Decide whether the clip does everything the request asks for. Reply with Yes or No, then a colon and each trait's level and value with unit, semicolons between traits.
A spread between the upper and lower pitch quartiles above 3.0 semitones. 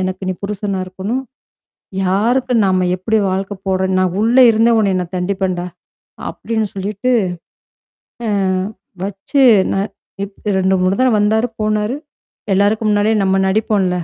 No: average, 2.7 semitones